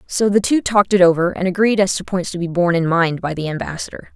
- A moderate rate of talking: No, fast, 275 wpm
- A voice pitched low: No, medium, 185 Hz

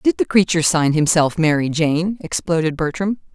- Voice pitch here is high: No, medium, 165 Hz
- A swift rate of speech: No, average, 160 wpm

